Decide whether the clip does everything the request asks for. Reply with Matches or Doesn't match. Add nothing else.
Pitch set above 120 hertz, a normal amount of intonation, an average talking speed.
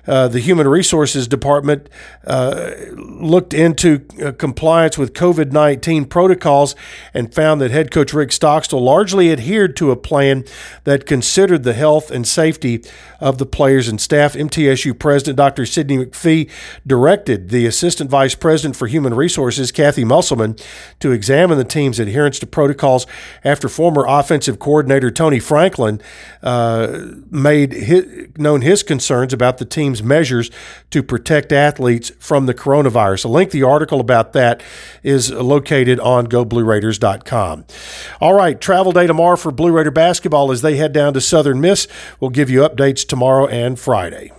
Matches